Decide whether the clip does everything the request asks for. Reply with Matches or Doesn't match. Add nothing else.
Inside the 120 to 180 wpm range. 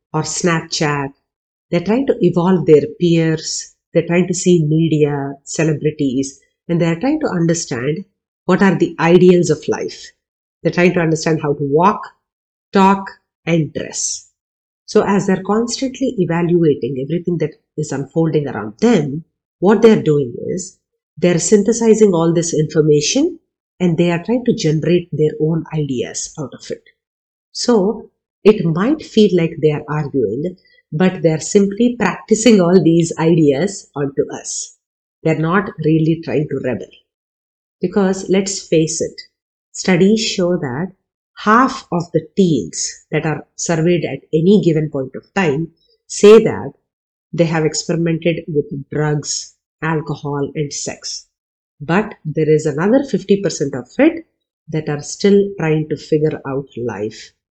Matches